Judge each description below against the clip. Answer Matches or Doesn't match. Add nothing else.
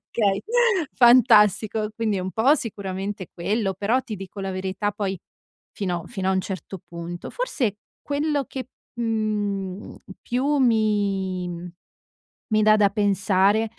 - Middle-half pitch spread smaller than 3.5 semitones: Matches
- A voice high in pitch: Matches